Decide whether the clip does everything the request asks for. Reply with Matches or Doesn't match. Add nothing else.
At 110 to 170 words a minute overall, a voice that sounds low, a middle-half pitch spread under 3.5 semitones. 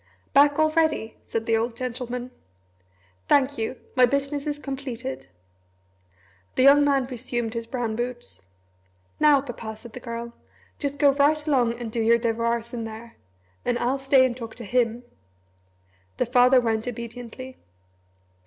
Doesn't match